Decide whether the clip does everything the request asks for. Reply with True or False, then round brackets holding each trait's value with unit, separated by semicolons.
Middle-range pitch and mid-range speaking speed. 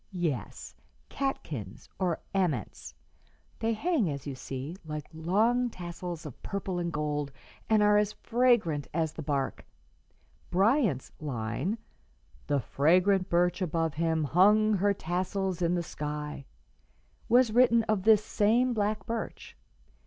False (180 Hz; 130 wpm)